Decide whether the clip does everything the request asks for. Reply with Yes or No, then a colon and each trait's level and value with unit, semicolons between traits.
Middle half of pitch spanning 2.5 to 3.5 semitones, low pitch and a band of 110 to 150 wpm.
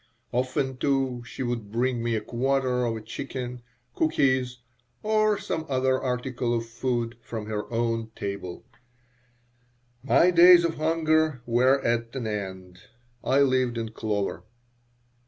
Yes: average, 2.8 semitones; low, 125 Hz; slow, 135 wpm